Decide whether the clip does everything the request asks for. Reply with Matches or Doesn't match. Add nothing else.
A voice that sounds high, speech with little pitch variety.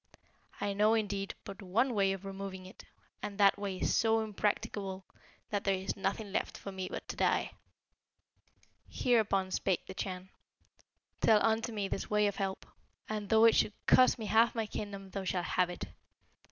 Matches